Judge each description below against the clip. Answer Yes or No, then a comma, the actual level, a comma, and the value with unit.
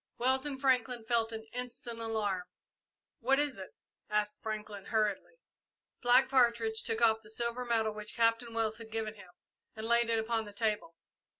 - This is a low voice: No, high, 225 Hz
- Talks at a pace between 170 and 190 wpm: Yes, average, 175 wpm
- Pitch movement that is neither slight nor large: No, narrow, 1.6 semitones